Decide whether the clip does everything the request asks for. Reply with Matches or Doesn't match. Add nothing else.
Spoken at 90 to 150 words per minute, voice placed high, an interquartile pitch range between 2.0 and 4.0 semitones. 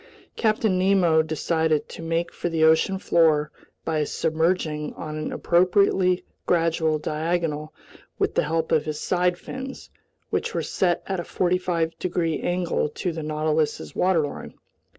Doesn't match